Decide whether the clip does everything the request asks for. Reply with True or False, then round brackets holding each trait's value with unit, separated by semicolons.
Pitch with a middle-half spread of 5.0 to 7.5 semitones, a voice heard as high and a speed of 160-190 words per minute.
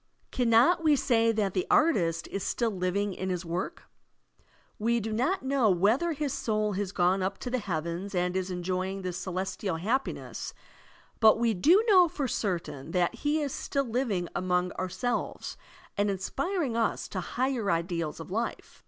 True (5.3 semitones; 205 Hz; 170 wpm)